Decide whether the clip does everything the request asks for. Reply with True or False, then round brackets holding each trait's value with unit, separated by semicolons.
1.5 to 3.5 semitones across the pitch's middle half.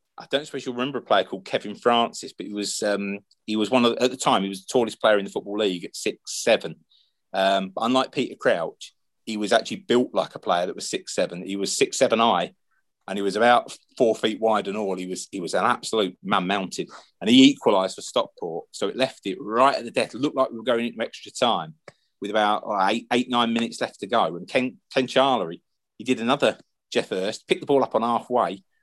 False (4.0 semitones)